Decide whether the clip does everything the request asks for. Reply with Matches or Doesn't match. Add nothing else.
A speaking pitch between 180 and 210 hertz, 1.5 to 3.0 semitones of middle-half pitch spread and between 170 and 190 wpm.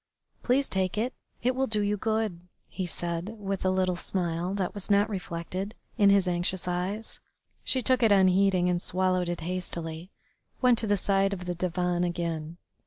Matches